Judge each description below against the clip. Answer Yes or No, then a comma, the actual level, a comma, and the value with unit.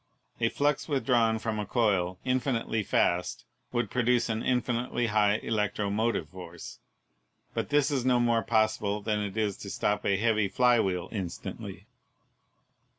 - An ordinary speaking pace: Yes, average, 150 wpm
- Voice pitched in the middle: No, low, 110 Hz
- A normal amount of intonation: Yes, average, 3.0 semitones